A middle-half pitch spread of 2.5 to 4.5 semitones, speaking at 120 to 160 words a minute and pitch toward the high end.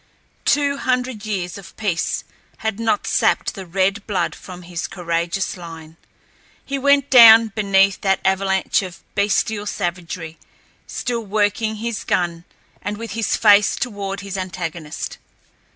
Yes: average, 3.5 semitones; slow, 135 wpm; high, 200 Hz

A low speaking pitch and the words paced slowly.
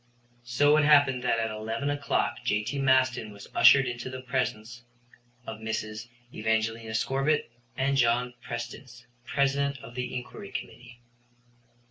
Yes: low, 125 Hz; slow, 130 wpm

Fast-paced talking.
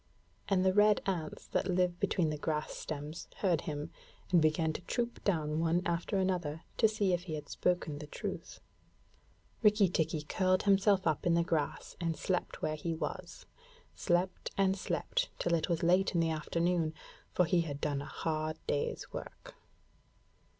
No: average, 170 wpm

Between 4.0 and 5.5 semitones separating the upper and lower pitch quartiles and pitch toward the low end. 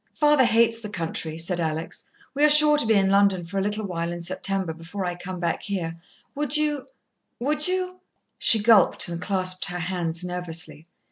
No: average, 5.2 semitones; high, 190 Hz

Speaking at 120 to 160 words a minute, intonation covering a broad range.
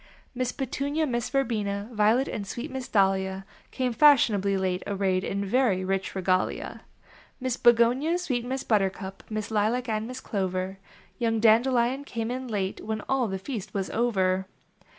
No: average, 150 wpm; average, 4.6 semitones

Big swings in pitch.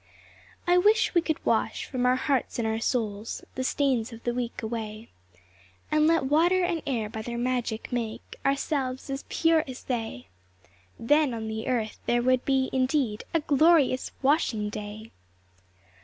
No: average, 4.4 semitones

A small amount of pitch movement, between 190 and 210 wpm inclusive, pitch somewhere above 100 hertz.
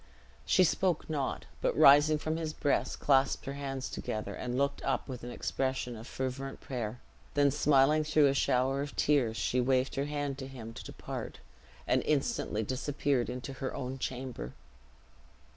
No: narrow, 2.3 semitones; average, 165 wpm; low, 135 Hz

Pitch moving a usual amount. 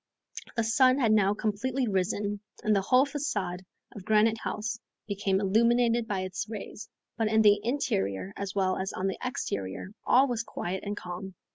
Yes: average, 3.3 semitones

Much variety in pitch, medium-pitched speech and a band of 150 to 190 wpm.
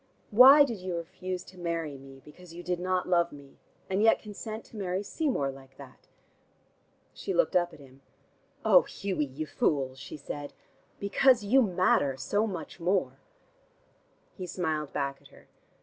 Yes: wide, 5.8 semitones; medium, 175 Hz; average, 165 wpm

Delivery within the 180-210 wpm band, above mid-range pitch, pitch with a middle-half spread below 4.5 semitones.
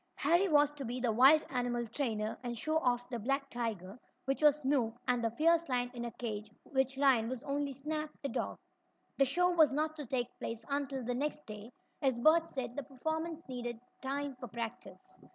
Yes: average, 200 wpm; very high, 265 Hz; average, 3.5 semitones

